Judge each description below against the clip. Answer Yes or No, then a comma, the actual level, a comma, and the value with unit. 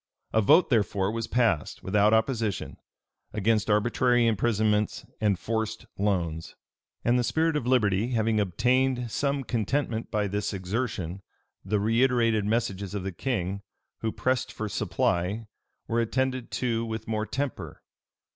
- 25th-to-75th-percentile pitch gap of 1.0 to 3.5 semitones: Yes, average, 3.1 semitones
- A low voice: Yes, low, 110 Hz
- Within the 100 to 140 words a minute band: Yes, slow, 135 wpm